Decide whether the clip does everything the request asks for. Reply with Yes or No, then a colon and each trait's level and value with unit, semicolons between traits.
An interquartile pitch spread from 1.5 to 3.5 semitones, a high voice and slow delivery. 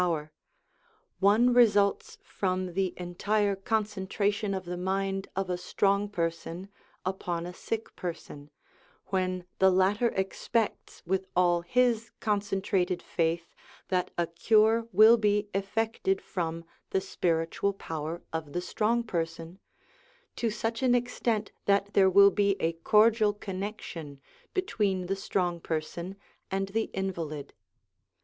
Yes: average, 3.0 semitones; high, 195 Hz; slow, 125 wpm